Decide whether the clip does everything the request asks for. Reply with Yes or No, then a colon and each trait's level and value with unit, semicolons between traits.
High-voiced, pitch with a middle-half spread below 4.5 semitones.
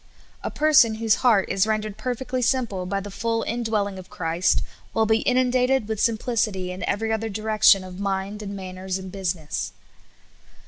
Yes: high, 215 Hz; average, 3.0 semitones